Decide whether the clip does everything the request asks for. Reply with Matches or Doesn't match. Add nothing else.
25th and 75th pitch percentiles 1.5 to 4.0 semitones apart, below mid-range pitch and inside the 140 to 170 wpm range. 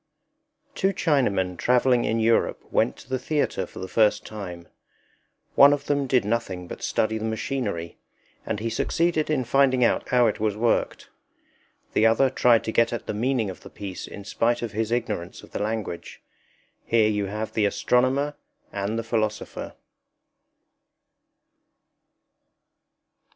Matches